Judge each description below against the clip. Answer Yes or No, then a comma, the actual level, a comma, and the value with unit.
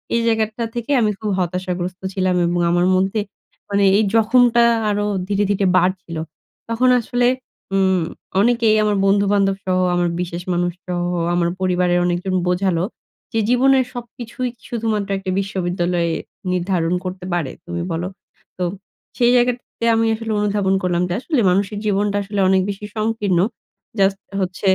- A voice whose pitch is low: No, high, 195 Hz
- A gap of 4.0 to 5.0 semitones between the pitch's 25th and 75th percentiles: No, average, 3.4 semitones